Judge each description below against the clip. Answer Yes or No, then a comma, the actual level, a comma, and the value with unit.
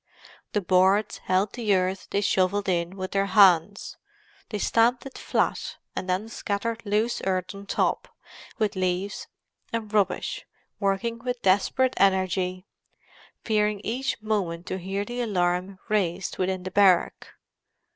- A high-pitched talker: Yes, high, 195 Hz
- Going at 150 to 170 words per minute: No, slow, 135 wpm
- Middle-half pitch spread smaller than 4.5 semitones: Yes, narrow, 2.5 semitones